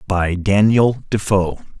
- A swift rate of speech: No, slow, 100 wpm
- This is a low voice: Yes, low, 100 Hz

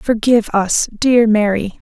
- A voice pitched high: Yes, high, 220 Hz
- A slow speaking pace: Yes, slow, 125 wpm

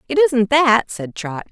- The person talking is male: No, female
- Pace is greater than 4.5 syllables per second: No, 3.9 syllables/s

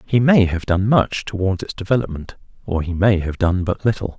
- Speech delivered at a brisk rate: Yes, fast, 215 wpm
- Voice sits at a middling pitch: No, low, 100 Hz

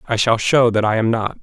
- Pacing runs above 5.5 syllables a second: Yes, 5.7 syllables/s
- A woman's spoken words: No, male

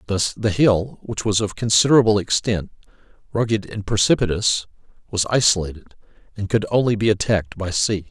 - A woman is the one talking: No, male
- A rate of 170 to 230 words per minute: No, average, 150 wpm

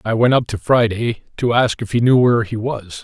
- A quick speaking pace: Yes, fast, 255 wpm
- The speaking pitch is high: No, low, 115 Hz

